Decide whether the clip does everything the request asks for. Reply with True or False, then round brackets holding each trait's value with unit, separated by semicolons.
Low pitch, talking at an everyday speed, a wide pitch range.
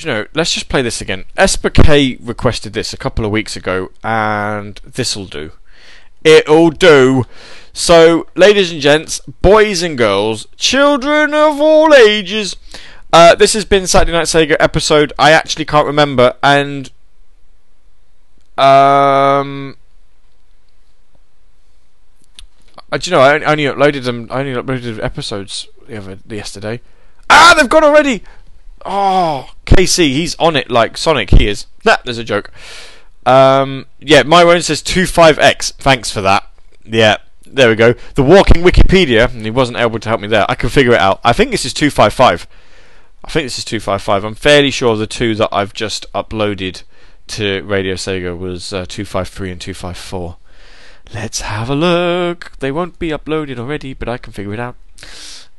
True (130 Hz; 170 wpm; 7.5 semitones)